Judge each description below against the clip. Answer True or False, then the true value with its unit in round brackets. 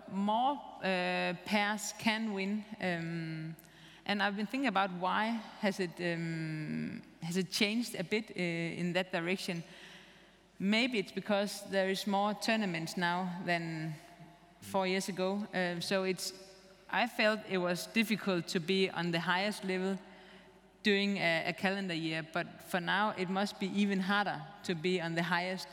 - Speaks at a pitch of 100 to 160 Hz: False (190 Hz)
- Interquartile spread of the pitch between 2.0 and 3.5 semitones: True (2.5 semitones)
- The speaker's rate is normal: True (160 wpm)